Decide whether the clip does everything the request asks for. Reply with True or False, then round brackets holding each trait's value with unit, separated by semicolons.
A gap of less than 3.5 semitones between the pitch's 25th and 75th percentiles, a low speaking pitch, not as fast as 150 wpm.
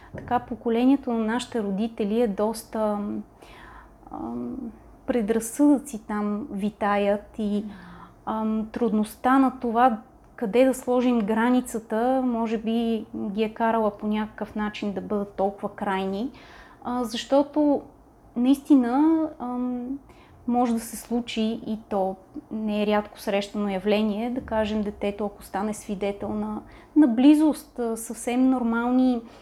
False (2.8 semitones; 225 Hz; 120 wpm)